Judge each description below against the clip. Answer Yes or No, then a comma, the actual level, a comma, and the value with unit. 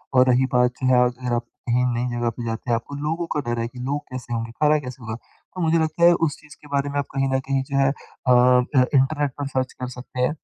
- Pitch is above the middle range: No, low, 130 Hz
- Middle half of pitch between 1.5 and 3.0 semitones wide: Yes, narrow, 2.5 semitones